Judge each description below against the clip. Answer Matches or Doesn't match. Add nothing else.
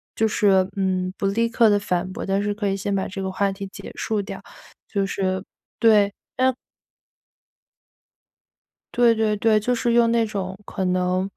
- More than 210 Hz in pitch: Doesn't match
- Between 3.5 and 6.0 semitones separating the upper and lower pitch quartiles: Doesn't match